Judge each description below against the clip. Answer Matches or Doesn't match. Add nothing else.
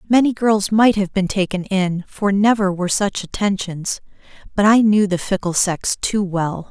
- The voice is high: Matches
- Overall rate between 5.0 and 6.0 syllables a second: Doesn't match